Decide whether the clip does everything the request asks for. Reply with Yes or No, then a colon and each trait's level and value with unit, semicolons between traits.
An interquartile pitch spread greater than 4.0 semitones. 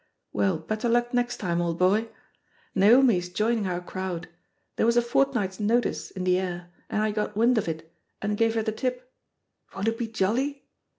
Yes: average, 4.4 semitones